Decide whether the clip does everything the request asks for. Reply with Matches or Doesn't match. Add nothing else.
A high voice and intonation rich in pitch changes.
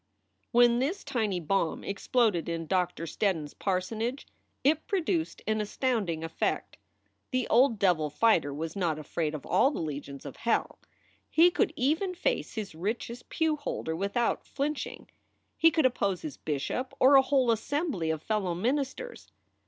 Matches